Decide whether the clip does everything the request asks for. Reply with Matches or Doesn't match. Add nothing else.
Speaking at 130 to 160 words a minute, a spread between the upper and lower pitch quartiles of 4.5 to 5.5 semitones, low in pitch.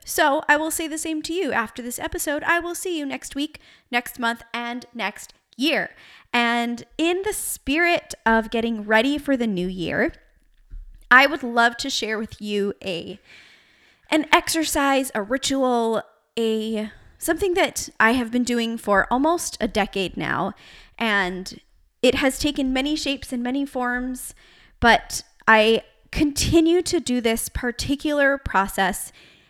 Doesn't match